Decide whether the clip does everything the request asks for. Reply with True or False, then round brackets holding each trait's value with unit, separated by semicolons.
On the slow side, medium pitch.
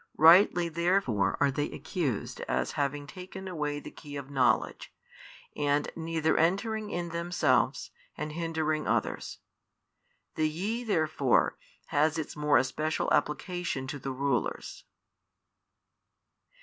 True (115 wpm; 155 Hz)